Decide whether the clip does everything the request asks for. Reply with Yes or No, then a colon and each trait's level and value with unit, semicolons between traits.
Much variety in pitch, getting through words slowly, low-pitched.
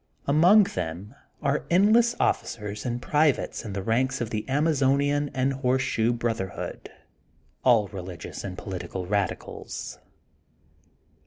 Yes: wide, 6.0 semitones; slow, 115 wpm; low, 125 Hz